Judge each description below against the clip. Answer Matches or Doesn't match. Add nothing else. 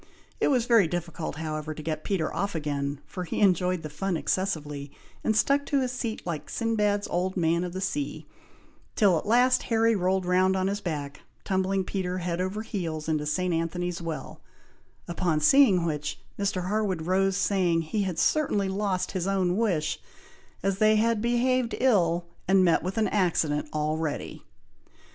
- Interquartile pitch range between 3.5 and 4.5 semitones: Matches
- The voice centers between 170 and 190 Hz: Matches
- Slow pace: Doesn't match